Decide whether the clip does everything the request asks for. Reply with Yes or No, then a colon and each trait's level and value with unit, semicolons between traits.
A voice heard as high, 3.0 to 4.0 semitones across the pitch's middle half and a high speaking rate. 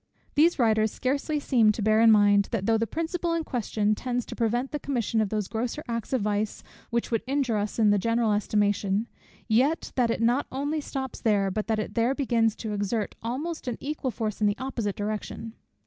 Yes: high, 230 Hz; average, 3.6 semitones; fast, 210 wpm